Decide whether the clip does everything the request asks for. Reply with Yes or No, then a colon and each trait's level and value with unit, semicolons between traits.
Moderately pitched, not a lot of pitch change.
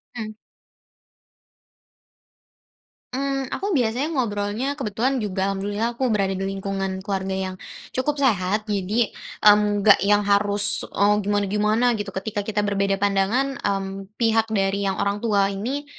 No: high, 205 Hz; narrow, 2.3 semitones